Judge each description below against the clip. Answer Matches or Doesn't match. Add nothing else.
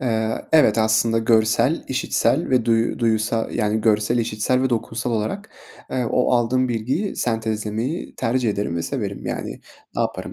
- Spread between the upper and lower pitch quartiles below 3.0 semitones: Matches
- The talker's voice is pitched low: Matches